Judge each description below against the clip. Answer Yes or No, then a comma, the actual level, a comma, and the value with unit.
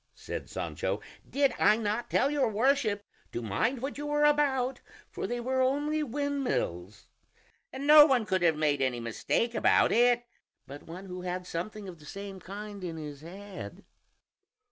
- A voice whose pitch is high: Yes, high, 215 Hz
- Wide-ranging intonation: Yes, wide, 7.3 semitones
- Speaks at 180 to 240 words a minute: No, average, 165 wpm